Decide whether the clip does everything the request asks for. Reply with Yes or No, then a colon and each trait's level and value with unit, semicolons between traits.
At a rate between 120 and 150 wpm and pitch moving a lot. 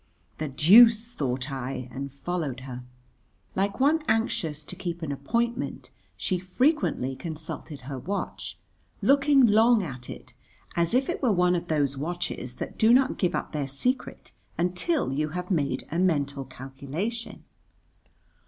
Yes: average, 145 wpm; wide, 8.3 semitones